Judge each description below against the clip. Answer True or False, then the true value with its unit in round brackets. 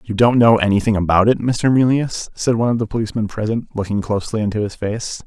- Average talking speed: False (215 wpm)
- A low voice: True (110 Hz)